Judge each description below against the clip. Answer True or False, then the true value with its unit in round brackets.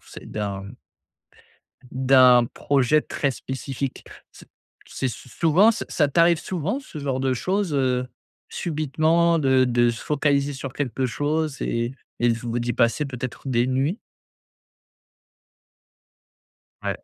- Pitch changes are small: False (3.6 semitones)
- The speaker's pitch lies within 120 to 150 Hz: True (135 Hz)